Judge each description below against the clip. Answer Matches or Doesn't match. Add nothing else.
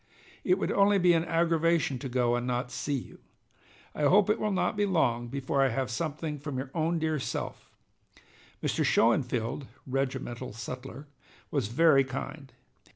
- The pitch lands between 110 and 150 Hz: Matches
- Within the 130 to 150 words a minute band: Doesn't match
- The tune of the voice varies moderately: Matches